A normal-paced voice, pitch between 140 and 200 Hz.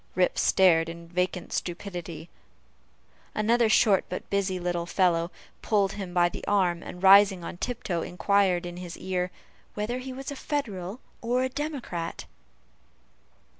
No: slow, 130 wpm; medium, 185 Hz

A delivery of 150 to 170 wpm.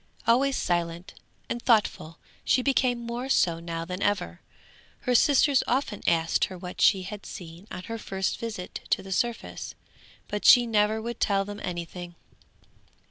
Yes: average, 155 wpm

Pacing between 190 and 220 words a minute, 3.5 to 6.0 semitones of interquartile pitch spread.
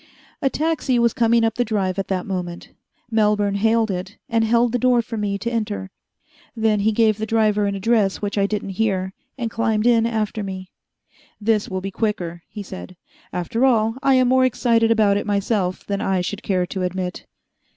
No: average, 195 wpm; average, 2.8 semitones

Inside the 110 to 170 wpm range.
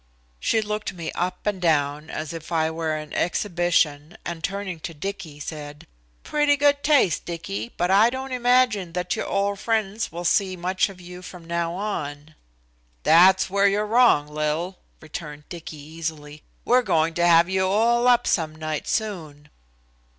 Yes: average, 165 wpm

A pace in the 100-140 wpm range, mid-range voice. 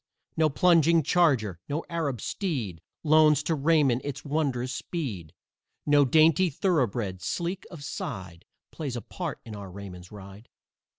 Yes: slow, 135 wpm; medium, 145 Hz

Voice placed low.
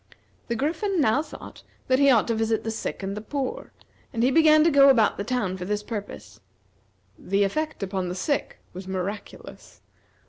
No: high, 225 Hz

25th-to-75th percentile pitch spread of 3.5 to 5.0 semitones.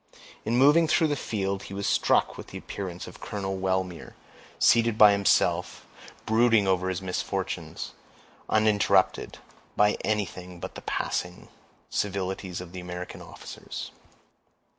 No: average, 2.8 semitones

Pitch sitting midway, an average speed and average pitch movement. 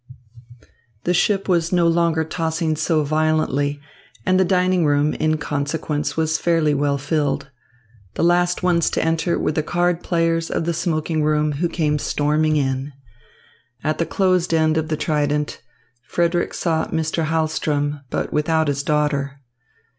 No: medium, 155 Hz; average, 150 wpm; narrow, 2.2 semitones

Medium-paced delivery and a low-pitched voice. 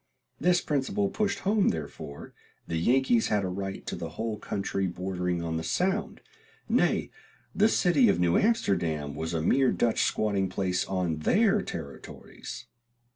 Yes: average, 150 wpm; very low, 95 Hz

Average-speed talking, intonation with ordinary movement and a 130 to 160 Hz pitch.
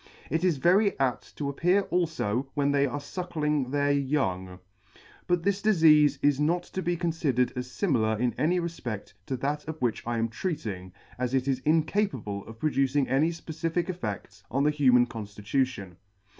Yes: average, 170 wpm; average, 5.0 semitones; medium, 140 Hz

